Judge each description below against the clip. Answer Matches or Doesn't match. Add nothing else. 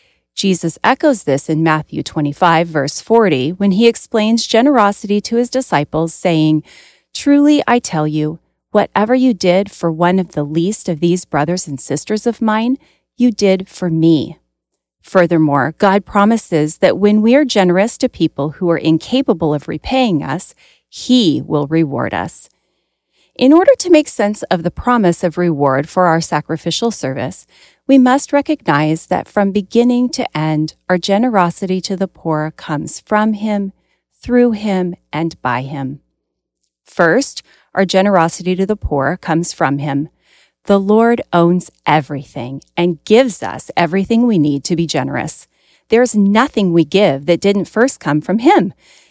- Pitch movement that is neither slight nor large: Doesn't match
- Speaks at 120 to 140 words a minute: Doesn't match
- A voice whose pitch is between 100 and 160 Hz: Doesn't match